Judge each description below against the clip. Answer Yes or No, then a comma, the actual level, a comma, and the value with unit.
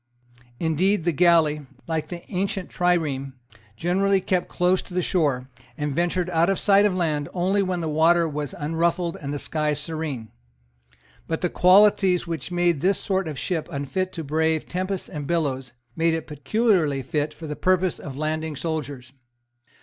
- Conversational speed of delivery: Yes, average, 165 wpm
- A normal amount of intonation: Yes, average, 3.3 semitones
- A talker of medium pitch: Yes, medium, 165 Hz